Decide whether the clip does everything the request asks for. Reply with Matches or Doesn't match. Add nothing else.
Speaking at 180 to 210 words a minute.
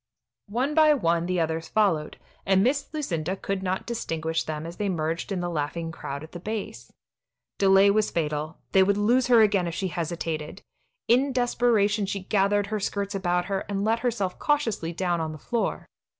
Matches